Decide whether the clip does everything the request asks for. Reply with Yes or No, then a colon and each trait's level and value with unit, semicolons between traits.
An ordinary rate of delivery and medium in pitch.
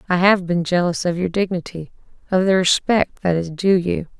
Yes: average, 185 wpm; medium, 180 Hz